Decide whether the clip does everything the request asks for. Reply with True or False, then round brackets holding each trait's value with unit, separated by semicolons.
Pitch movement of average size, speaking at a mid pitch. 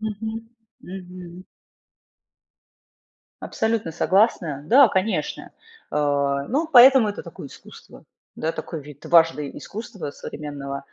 False (6.9 semitones; 180 Hz)